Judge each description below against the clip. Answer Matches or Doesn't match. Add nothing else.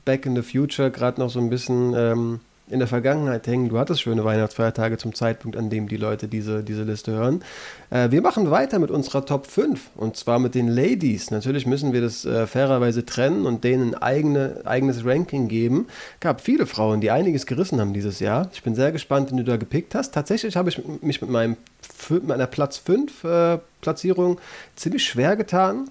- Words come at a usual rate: Doesn't match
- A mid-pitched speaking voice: Doesn't match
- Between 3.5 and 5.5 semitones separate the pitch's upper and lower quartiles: Matches